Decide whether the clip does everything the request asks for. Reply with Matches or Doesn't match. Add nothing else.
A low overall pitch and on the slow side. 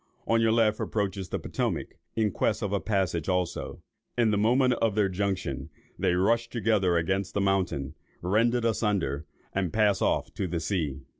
Doesn't match